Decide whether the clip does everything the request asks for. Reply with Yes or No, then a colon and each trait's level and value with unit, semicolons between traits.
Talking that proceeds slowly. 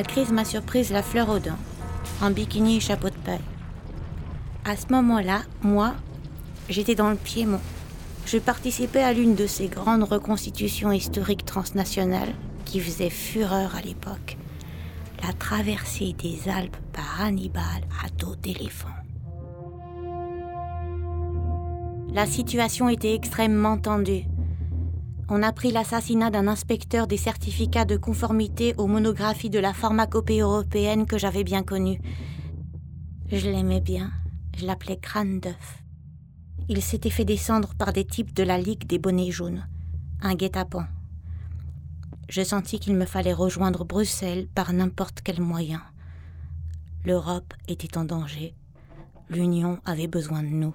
Yes: slow, 135 wpm